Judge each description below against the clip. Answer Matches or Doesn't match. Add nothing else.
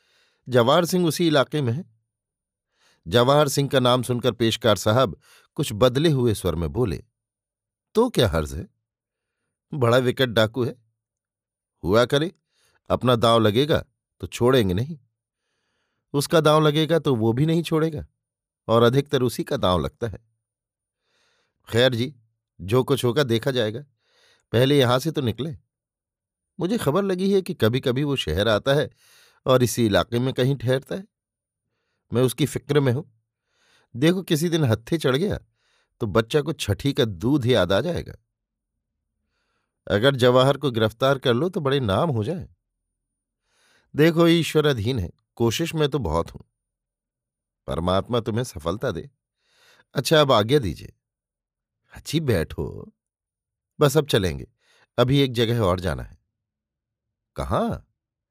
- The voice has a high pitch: Doesn't match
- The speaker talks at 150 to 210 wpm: Doesn't match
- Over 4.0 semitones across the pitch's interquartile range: Matches